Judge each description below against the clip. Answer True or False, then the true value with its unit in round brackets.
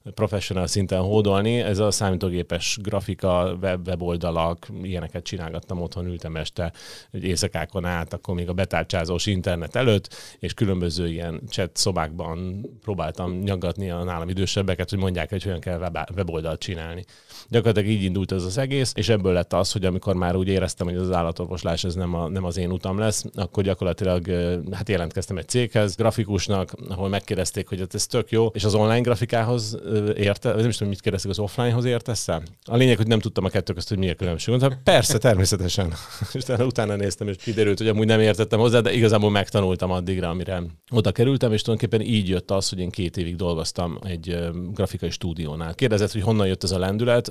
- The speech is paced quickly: True (185 wpm)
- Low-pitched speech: True (95 Hz)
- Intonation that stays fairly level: False (3.2 semitones)